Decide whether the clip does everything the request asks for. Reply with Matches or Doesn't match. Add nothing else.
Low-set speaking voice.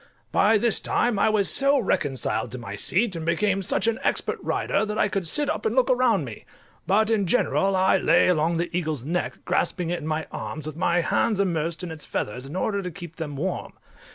Doesn't match